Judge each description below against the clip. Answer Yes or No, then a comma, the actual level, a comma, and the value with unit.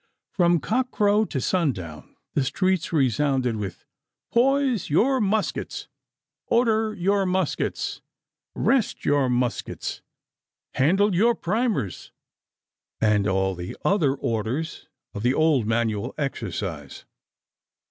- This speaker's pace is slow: Yes, slow, 105 wpm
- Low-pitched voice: No, medium, 155 Hz